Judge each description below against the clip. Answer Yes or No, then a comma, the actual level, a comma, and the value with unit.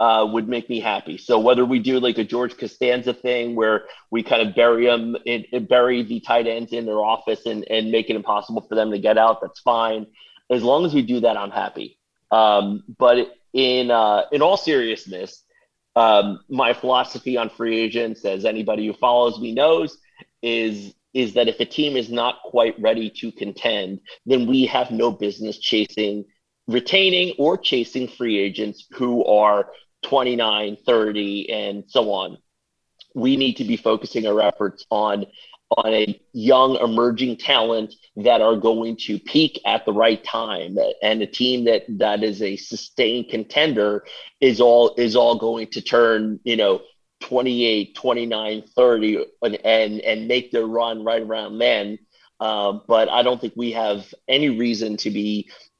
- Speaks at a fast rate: No, average, 175 wpm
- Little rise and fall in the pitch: Yes, narrow, 2.3 semitones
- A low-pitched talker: Yes, low, 115 Hz